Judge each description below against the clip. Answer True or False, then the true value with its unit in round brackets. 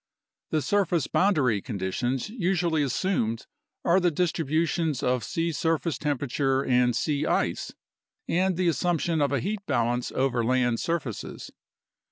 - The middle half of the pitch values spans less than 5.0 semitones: False (5.4 semitones)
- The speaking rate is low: True (130 wpm)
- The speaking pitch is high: False (145 Hz)